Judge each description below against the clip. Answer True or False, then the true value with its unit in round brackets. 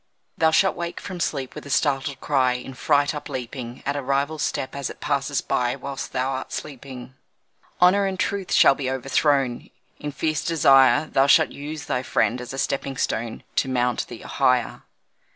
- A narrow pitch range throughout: True (2.3 semitones)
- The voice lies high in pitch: False (135 Hz)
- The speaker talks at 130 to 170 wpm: False (180 wpm)